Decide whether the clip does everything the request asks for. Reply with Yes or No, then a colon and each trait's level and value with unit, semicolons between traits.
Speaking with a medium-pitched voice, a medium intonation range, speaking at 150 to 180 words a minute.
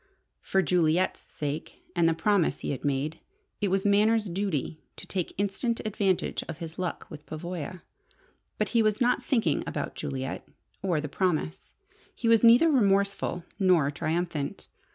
Yes: medium, 180 Hz; average, 4.6 semitones; average, 155 wpm